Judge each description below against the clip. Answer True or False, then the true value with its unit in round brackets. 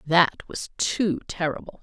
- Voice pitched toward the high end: False (170 Hz)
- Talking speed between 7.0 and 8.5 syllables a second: False (4.0 syllables/s)